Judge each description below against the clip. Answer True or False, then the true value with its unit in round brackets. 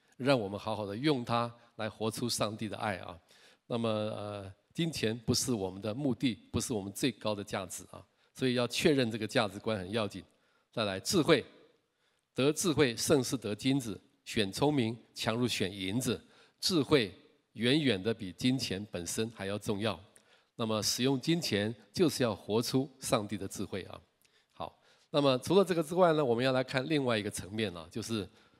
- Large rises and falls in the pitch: False (4.1 semitones)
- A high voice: False (115 Hz)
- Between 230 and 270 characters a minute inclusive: True (265 characters per minute)